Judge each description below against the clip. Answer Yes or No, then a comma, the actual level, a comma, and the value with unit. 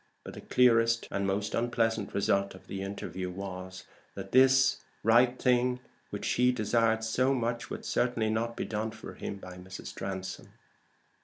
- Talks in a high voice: No, low, 110 Hz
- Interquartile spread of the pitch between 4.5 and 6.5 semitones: No, average, 3.6 semitones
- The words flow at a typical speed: Yes, average, 160 wpm